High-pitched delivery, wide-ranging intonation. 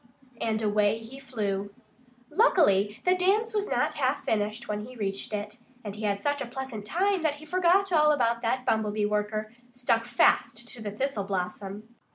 Yes: high, 225 Hz; wide, 5.7 semitones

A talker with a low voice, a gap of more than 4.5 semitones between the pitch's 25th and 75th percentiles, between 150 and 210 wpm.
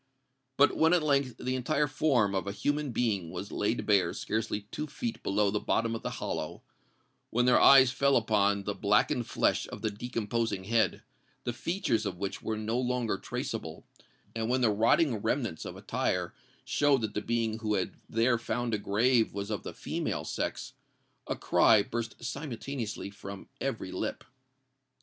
No: low, 115 Hz; average, 3.6 semitones; average, 170 wpm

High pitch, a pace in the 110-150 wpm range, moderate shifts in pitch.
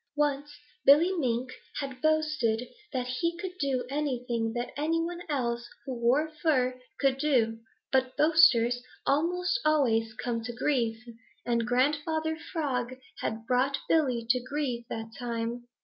Yes: very high, 260 Hz; slow, 135 wpm; average, 4.0 semitones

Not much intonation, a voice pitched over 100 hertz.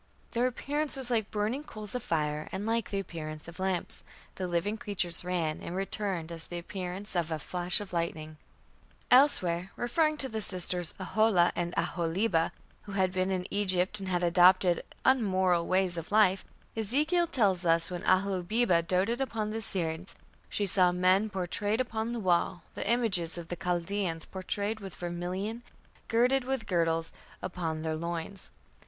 No: average, 3.8 semitones; medium, 185 Hz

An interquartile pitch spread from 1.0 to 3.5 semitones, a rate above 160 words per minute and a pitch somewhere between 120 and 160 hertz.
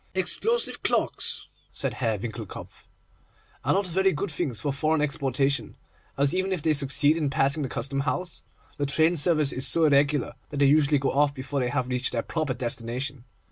Yes: average, 3.0 semitones; average, 180 wpm; medium, 140 Hz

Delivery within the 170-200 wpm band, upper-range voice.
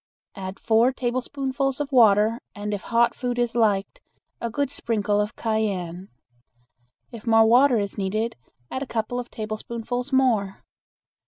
No: average, 145 wpm; high, 230 Hz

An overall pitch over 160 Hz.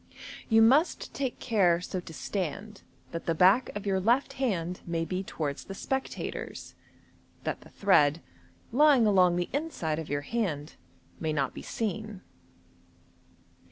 Yes: high, 190 Hz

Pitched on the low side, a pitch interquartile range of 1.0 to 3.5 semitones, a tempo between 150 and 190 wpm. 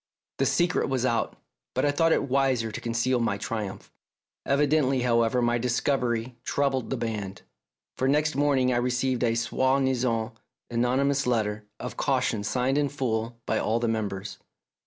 Yes: low, 125 Hz; average, 2.7 semitones; average, 155 wpm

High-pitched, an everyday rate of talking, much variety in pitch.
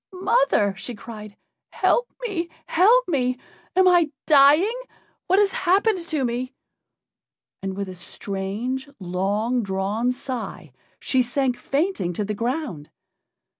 No: very high, 250 Hz; slow, 125 wpm; wide, 9.0 semitones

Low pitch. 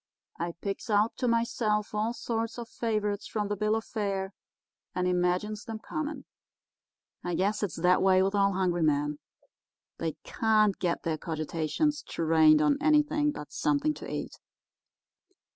No: high, 205 Hz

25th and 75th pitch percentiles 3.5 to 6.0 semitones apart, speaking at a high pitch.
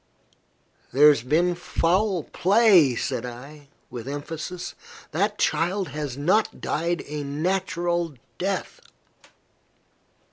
No: average, 4.2 semitones; medium, 165 Hz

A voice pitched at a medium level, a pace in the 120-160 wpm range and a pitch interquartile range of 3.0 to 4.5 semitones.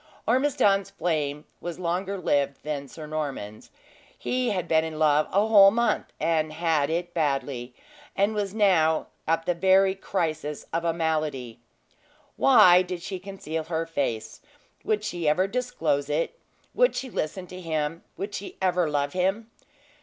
Yes: medium, 165 Hz; average, 155 wpm; average, 4.2 semitones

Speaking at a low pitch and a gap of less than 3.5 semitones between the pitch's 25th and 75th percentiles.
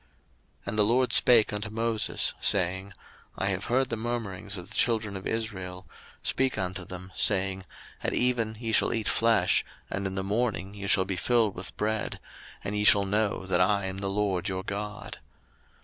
Yes: low, 100 Hz; average, 2.7 semitones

